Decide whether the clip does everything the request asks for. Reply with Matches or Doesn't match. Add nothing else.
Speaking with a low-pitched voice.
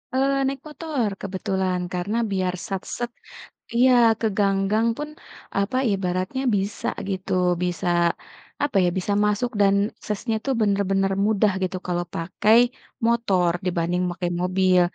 Doesn't match